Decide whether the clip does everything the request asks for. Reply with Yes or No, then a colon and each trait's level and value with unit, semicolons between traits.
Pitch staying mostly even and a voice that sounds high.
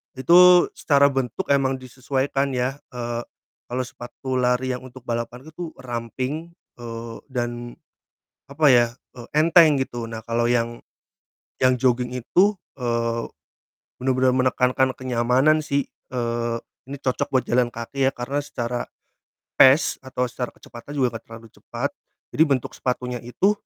No: narrow, 2.3 semitones; low, 125 Hz